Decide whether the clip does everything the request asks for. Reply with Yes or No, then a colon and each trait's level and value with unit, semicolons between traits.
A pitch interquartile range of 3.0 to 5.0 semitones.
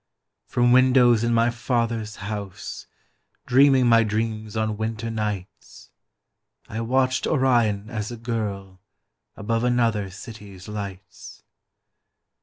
No: narrow, 2.4 semitones